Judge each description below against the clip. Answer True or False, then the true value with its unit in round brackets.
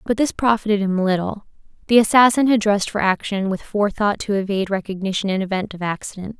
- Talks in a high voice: True (205 Hz)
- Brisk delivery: False (190 wpm)